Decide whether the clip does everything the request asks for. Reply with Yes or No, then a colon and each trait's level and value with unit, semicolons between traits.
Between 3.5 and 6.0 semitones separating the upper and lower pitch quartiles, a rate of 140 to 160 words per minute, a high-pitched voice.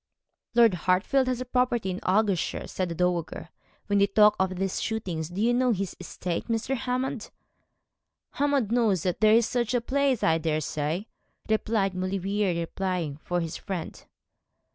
Yes: average, 4.7 semitones; average, 155 wpm; high, 195 Hz